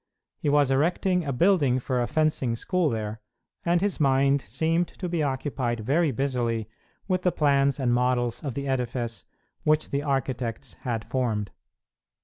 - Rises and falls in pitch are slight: No, average, 4.1 semitones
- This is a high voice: No, low, 135 Hz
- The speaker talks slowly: No, average, 155 wpm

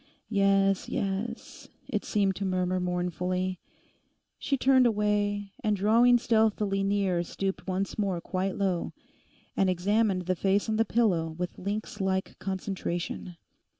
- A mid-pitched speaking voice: No, high, 195 Hz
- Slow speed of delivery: Yes, slow, 130 wpm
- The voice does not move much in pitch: Yes, narrow, 2.2 semitones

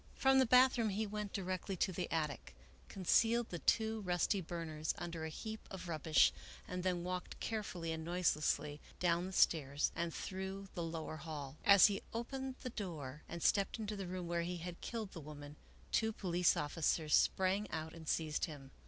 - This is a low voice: No, medium, 175 Hz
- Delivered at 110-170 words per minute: No, average, 180 wpm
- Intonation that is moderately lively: Yes, average, 4.0 semitones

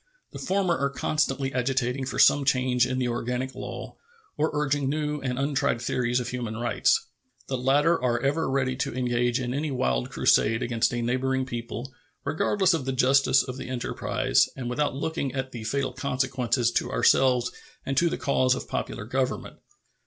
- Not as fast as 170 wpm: No, average, 175 wpm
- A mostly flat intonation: Yes, narrow, 2.1 semitones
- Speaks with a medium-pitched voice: No, low, 130 Hz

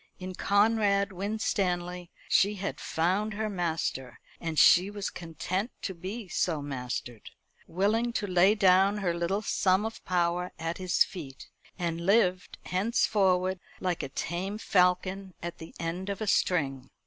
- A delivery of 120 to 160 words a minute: Yes, average, 145 wpm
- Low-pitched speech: No, medium, 185 Hz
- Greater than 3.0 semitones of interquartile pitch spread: No, average, 2.7 semitones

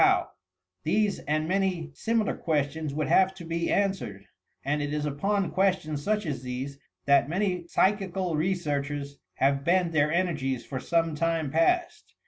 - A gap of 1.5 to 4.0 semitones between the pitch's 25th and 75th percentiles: No, average, 4.7 semitones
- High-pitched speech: No, medium, 165 Hz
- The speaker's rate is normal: Yes, average, 150 wpm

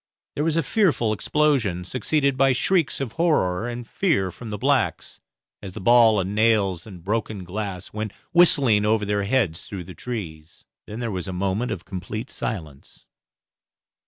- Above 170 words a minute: No, average, 165 wpm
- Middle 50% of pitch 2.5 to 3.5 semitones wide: No, average, 4.8 semitones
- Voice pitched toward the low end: Yes, low, 110 Hz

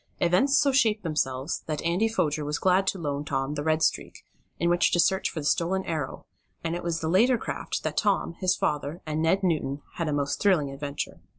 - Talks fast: Yes, fast, 220 wpm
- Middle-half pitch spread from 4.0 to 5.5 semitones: Yes, average, 4.3 semitones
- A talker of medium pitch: Yes, medium, 165 Hz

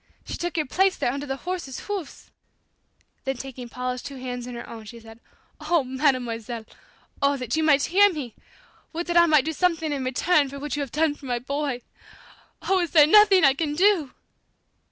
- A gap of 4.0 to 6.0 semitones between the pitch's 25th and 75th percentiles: Yes, average, 4.7 semitones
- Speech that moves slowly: No, average, 200 wpm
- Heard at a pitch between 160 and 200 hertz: No, very high, 285 Hz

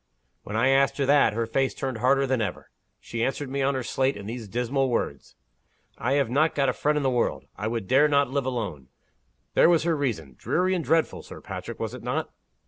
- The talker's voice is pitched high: No, low, 135 Hz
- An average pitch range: Yes, average, 3.4 semitones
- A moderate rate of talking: No, fast, 220 wpm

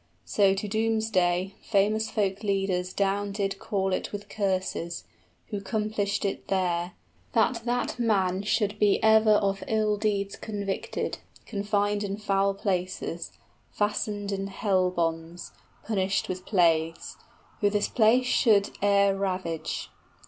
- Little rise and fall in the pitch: Yes, narrow, 2.0 semitones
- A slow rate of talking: Yes, slow, 130 wpm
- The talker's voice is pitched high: Yes, high, 200 Hz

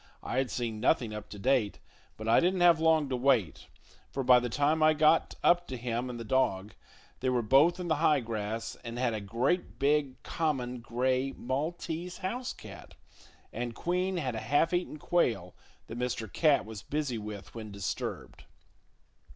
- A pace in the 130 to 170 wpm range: No, average, 180 wpm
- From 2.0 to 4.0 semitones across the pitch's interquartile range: No, wide, 5.4 semitones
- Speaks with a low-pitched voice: Yes, low, 130 Hz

